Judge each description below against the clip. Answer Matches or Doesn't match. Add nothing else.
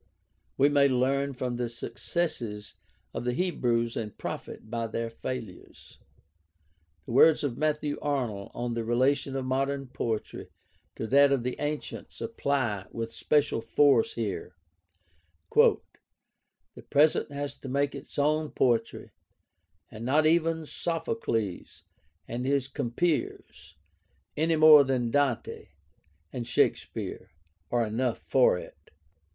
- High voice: Doesn't match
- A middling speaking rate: Doesn't match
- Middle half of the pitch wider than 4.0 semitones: Doesn't match